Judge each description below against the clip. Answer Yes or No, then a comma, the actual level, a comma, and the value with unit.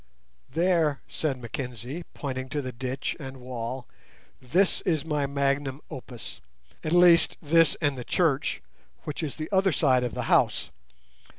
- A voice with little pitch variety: No, average, 3.8 semitones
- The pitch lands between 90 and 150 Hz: Yes, medium, 140 Hz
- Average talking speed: Yes, average, 155 wpm